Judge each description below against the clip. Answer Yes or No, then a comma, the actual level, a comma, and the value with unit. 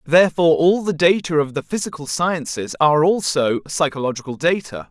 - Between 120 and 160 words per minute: Yes, average, 145 wpm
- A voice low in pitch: No, medium, 160 Hz